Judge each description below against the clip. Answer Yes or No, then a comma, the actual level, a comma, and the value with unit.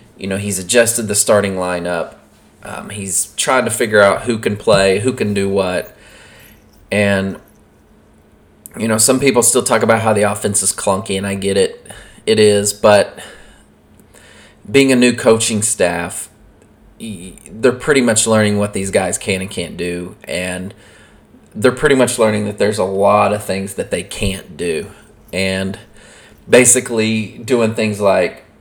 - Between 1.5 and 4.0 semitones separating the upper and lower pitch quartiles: Yes, narrow, 2.5 semitones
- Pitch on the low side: Yes, low, 105 Hz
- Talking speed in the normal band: Yes, average, 160 wpm